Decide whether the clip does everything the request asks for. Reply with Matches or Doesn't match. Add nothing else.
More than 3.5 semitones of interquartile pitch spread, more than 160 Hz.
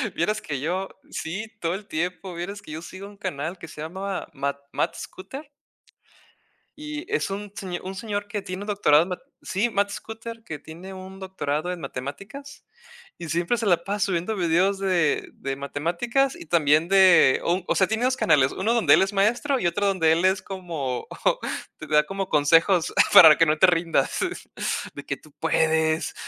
Matches